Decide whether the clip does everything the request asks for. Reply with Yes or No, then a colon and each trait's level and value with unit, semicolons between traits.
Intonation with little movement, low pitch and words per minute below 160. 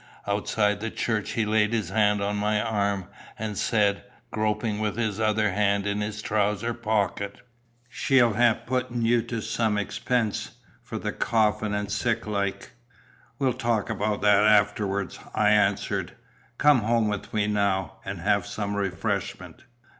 Yes: narrow, 1.7 semitones; low, 105 Hz; average, 150 wpm